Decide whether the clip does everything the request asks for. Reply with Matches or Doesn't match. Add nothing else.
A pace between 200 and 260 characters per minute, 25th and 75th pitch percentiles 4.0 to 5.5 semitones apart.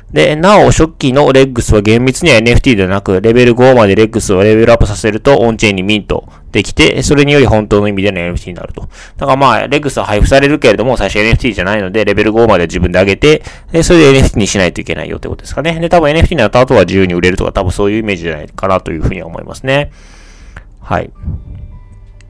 Doesn't match